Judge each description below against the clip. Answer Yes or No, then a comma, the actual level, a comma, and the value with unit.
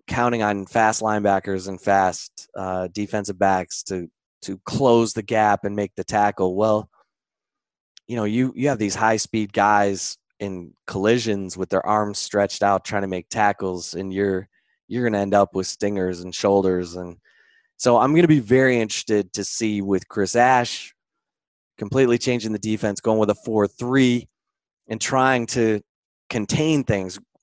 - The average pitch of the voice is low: Yes, low, 105 Hz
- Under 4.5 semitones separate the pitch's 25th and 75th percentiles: Yes, narrow, 2.6 semitones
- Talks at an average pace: Yes, average, 165 wpm